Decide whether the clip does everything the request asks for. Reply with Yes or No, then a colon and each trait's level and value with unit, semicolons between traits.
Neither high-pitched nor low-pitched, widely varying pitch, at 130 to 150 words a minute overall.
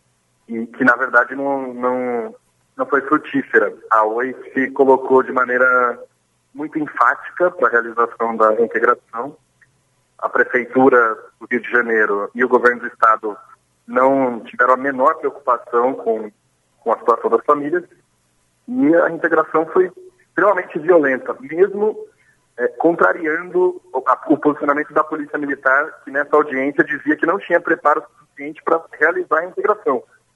Yes: medium, 145 Hz; wide, 8.9 semitones; average, 145 wpm